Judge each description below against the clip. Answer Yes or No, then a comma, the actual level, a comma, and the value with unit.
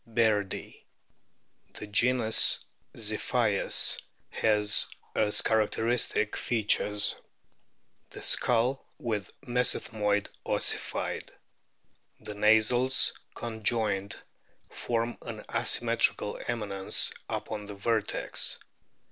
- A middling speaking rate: No, slow, 75 wpm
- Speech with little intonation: Yes, narrow, 2.2 semitones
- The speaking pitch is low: Yes, low, 110 Hz